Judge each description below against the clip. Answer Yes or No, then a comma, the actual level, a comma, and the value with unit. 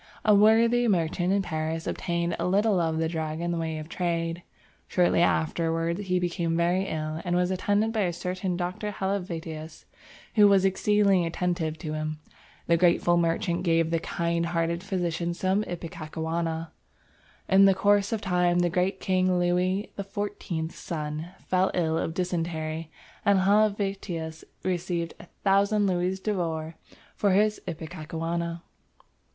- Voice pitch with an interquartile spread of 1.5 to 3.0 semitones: Yes, narrow, 2.6 semitones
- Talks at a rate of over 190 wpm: No, average, 145 wpm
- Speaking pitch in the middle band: Yes, medium, 175 Hz